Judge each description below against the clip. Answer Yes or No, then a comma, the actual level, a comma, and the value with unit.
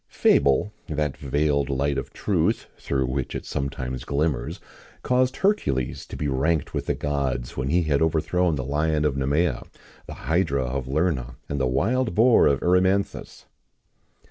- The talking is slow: No, average, 165 wpm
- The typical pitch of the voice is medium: No, very low, 70 Hz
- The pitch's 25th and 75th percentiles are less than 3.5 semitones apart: No, average, 4.1 semitones